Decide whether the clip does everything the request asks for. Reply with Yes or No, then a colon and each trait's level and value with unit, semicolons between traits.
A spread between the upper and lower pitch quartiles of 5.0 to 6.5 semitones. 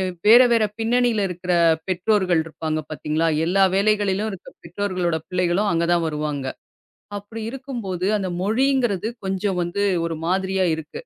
No: average, 3.7 semitones